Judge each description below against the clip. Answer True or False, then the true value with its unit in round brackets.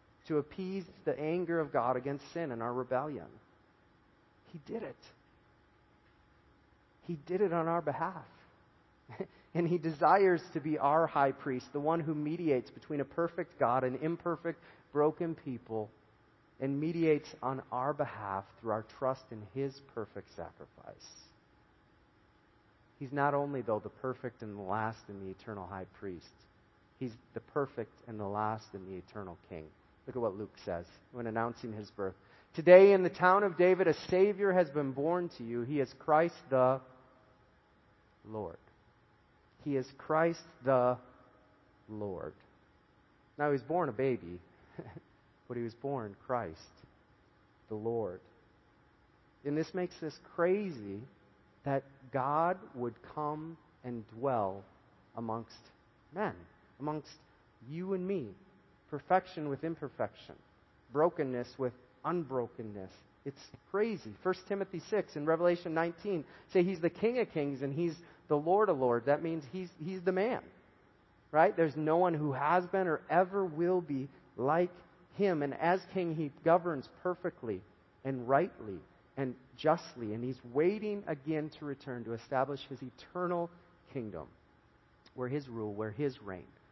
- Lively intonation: True (6.5 semitones)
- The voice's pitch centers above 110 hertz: True (140 Hz)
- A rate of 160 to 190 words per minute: False (145 wpm)